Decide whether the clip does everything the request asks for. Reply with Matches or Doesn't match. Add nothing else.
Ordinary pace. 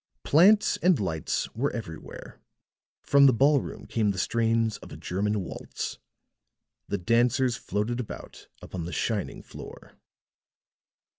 Doesn't match